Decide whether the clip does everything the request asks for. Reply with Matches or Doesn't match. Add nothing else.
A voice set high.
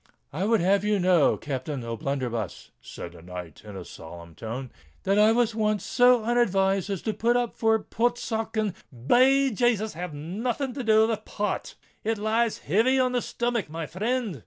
Matches